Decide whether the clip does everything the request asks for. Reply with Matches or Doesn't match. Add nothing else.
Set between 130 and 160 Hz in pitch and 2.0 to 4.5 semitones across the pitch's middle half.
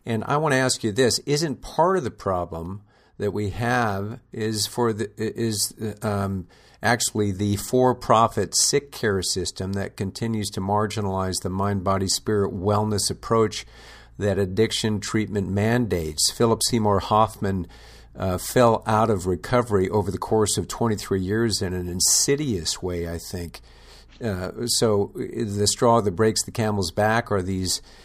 Doesn't match